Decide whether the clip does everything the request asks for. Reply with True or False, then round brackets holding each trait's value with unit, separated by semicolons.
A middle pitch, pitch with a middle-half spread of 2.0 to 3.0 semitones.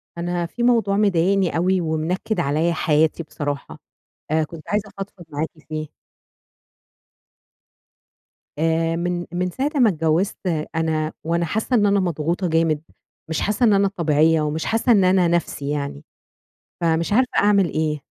False (170 Hz; 3.8 semitones)